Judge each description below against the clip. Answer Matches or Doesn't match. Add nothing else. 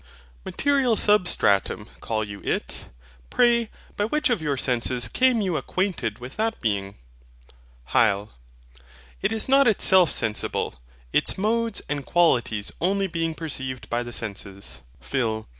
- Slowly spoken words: Matches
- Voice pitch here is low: Doesn't match